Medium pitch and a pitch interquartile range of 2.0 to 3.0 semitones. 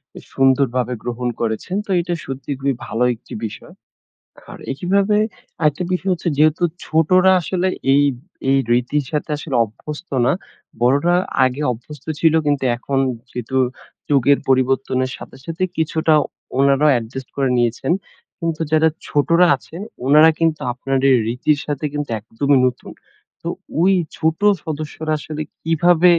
No: medium, 145 Hz; average, 3.6 semitones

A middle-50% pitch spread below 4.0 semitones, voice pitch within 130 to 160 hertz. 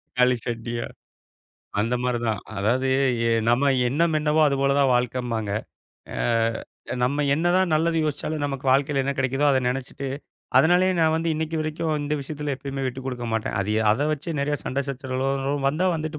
Yes: average, 3.5 semitones; medium, 140 Hz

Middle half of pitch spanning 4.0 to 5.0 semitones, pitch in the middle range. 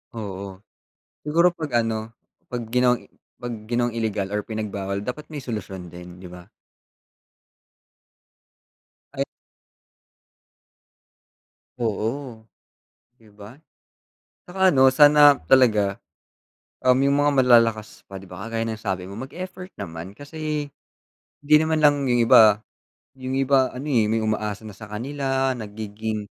No: average, 4.6 semitones; low, 115 Hz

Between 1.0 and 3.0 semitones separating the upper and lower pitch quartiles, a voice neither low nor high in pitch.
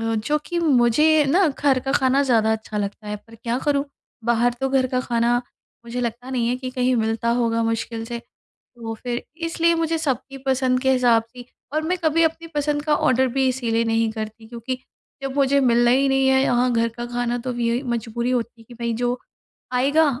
No: average, 2.7 semitones; very high, 250 Hz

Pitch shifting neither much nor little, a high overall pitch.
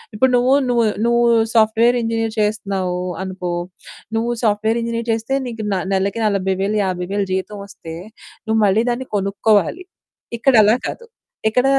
Yes: average, 3.0 semitones; high, 220 Hz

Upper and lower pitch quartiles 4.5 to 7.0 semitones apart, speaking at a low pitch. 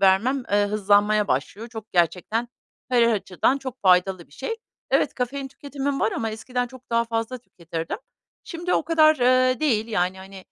No: average, 5.0 semitones; high, 225 Hz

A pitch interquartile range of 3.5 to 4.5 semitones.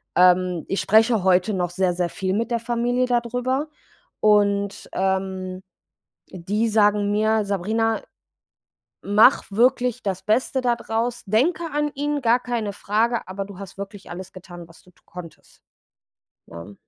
Yes: average, 4.0 semitones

